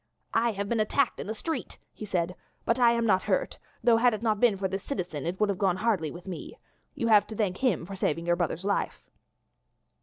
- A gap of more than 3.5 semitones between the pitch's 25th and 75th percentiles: Yes, average, 4.1 semitones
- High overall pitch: Yes, high, 205 Hz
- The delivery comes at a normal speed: No, fast, 235 wpm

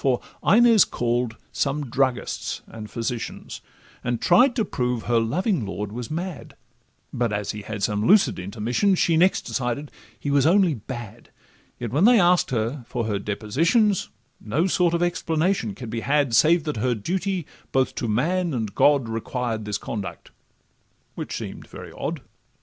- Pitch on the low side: Yes, low, 130 Hz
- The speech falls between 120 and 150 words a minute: No, average, 160 wpm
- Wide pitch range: Yes, wide, 7.2 semitones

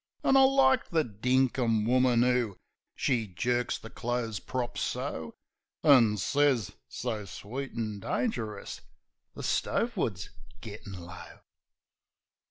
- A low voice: Yes, low, 120 Hz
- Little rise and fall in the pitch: No, average, 3.9 semitones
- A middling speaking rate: No, slow, 115 wpm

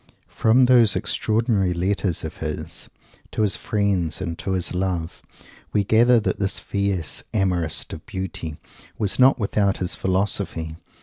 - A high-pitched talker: No, very low, 95 Hz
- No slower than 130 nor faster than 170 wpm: Yes, average, 140 wpm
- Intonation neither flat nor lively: Yes, average, 3.3 semitones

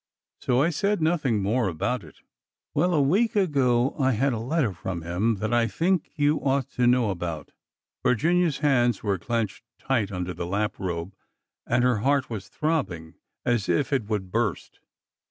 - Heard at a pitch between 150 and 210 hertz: No, low, 120 Hz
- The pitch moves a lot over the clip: Yes, wide, 6.2 semitones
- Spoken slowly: No, average, 170 wpm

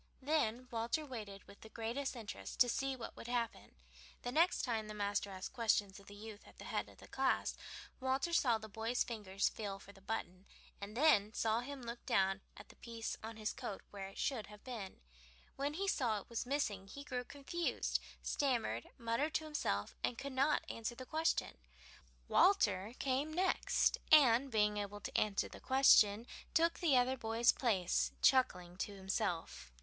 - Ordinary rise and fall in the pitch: Yes, average, 4.6 semitones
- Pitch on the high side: Yes, high, 230 Hz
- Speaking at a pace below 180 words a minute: No, average, 185 wpm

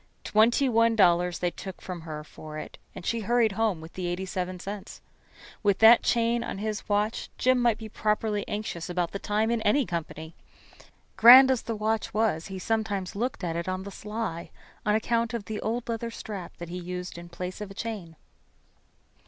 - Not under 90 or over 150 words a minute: No, average, 195 wpm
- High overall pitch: Yes, high, 210 Hz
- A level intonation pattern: No, average, 4.0 semitones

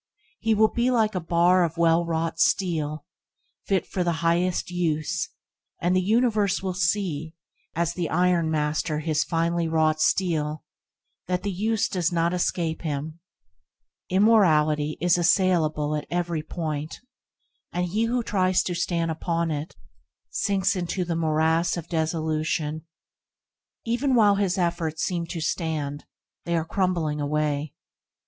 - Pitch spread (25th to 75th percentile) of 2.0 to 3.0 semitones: Yes, average, 2.7 semitones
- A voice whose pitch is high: No, medium, 170 Hz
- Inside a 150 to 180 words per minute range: No, average, 140 wpm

